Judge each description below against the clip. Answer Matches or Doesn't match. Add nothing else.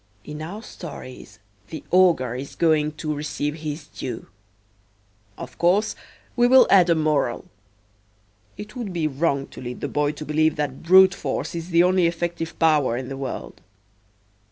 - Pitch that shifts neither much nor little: Matches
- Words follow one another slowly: Doesn't match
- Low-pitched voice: Doesn't match